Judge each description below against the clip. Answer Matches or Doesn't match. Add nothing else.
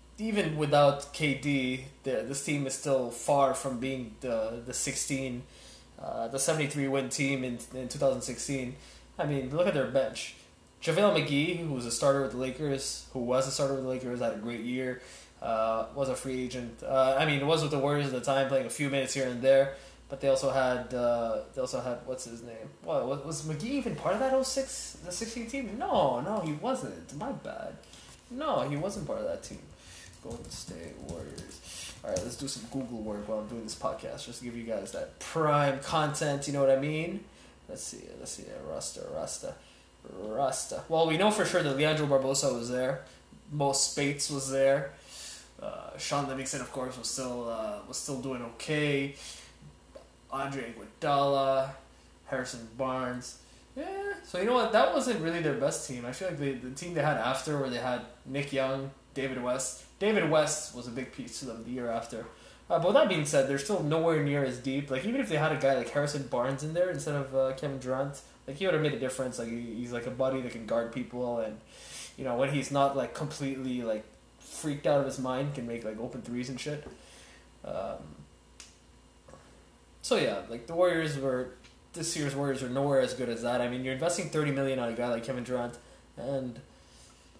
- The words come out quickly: Matches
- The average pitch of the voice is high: Doesn't match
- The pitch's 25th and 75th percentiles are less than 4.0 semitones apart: Matches